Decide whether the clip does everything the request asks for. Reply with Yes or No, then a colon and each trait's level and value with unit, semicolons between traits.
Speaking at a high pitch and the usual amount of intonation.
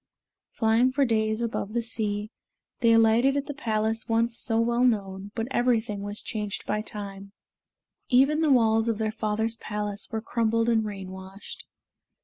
No: high, 220 Hz; narrow, 2.0 semitones